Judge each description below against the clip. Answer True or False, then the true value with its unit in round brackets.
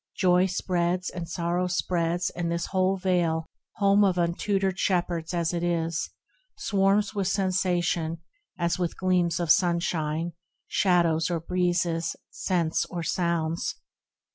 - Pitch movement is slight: True (1.6 semitones)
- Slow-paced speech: True (125 wpm)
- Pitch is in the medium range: True (175 Hz)